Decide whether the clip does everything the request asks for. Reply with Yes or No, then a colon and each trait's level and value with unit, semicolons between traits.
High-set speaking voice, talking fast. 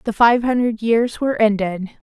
No: high, 225 Hz; average, 175 wpm